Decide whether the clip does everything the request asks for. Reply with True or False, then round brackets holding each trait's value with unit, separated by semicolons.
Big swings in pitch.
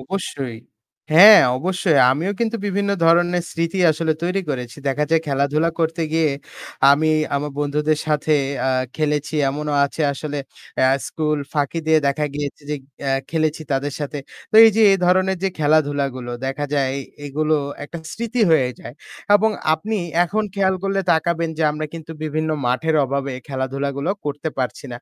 False (3.1 semitones)